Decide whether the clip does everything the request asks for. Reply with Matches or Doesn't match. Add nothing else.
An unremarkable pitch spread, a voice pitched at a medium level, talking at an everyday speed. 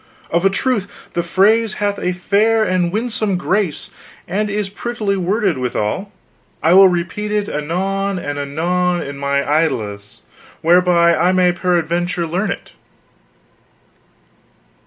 Doesn't match